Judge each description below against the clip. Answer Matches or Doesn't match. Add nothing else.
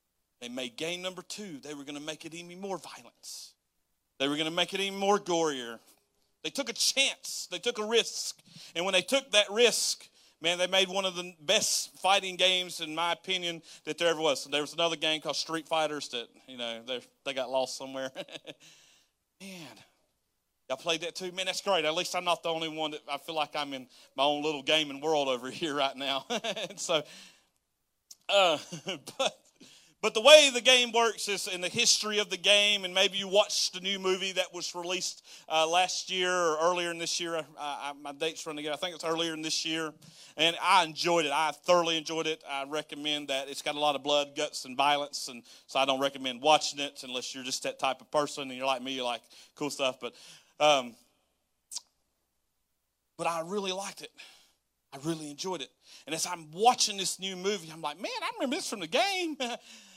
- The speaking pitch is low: Doesn't match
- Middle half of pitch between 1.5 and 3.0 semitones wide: Doesn't match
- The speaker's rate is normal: Doesn't match